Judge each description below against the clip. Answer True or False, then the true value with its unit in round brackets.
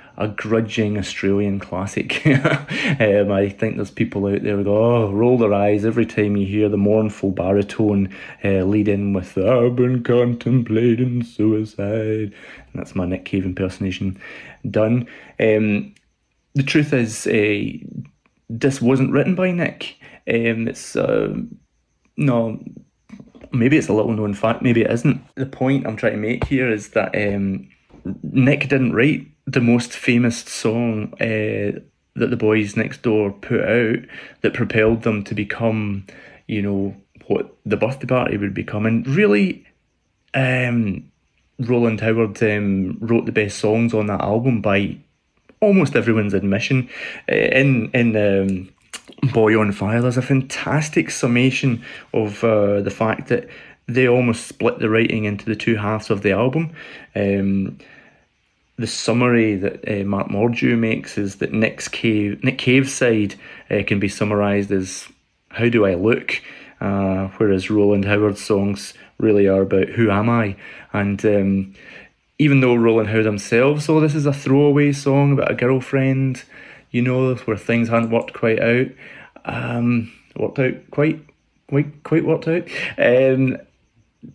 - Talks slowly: False (150 wpm)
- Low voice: True (110 Hz)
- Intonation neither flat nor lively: True (3.6 semitones)